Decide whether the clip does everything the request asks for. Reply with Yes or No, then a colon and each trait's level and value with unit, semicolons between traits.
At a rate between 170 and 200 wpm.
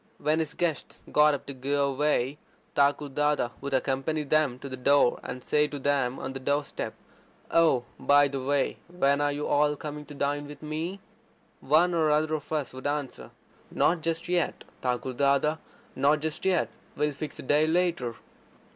Yes: average, 180 wpm